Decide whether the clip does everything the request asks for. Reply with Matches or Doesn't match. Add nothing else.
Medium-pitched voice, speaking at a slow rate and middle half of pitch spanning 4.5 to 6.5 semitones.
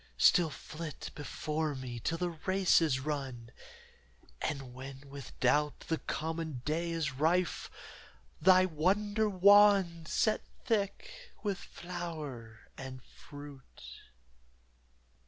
Matches